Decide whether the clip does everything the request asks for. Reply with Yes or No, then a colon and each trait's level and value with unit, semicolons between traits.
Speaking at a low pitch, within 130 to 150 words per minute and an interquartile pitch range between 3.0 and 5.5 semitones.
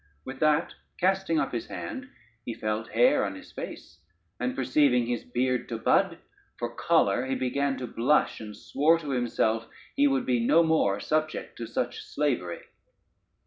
No: low, 125 Hz; average, 165 wpm; average, 4.3 semitones